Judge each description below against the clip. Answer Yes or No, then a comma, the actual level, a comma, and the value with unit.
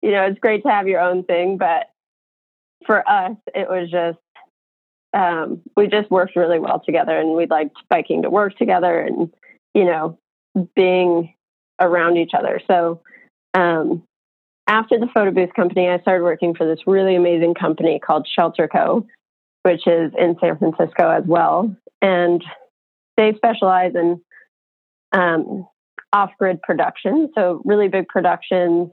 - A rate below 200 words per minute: Yes, average, 150 wpm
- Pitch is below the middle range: No, medium, 180 Hz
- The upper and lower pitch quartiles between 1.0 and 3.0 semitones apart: Yes, narrow, 2.4 semitones